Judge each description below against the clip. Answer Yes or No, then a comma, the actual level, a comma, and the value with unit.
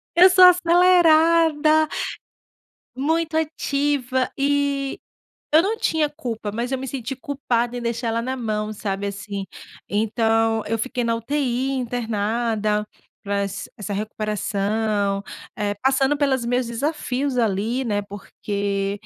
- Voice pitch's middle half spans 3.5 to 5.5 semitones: Yes, average, 5.1 semitones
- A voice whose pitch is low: No, high, 240 Hz